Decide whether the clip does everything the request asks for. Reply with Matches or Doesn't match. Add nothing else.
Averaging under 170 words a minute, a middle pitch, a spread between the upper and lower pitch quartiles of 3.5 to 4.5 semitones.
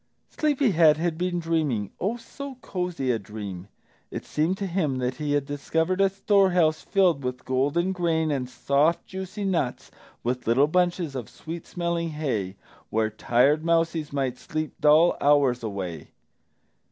Doesn't match